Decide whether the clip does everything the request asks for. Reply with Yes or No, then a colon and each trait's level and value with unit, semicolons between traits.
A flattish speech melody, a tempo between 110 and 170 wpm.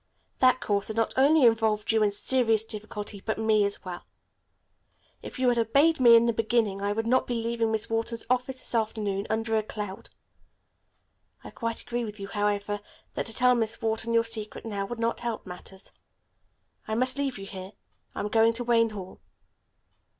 No: narrow, 2.2 semitones; average, 195 wpm